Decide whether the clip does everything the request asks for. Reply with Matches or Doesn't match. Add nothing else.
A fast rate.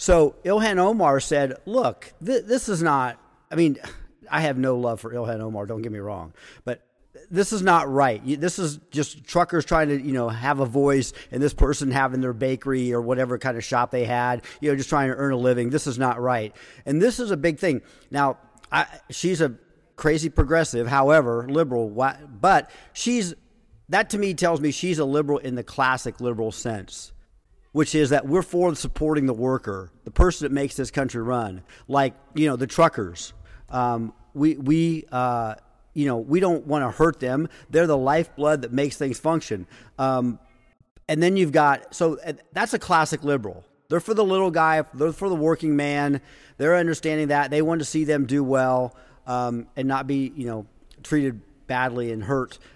Doesn't match